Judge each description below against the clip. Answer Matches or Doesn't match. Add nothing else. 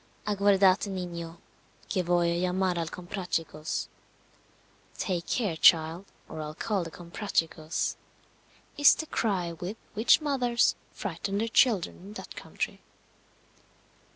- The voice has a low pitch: Doesn't match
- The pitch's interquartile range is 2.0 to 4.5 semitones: Matches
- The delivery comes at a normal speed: Doesn't match